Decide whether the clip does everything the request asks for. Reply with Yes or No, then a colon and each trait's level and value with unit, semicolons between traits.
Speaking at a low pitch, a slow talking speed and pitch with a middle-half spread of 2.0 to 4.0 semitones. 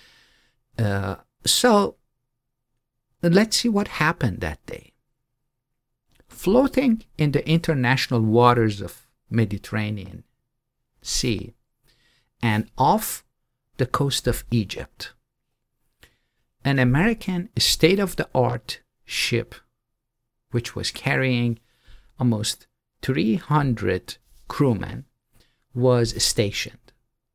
Yes: low, 125 Hz; slow, 75 wpm; average, 2.7 semitones